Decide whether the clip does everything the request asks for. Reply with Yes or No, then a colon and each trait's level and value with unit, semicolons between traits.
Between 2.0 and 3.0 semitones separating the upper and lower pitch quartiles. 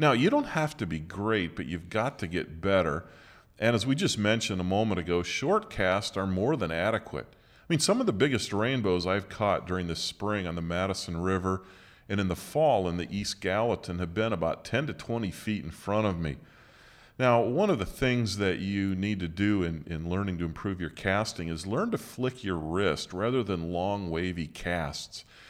No: average, 3.9 semitones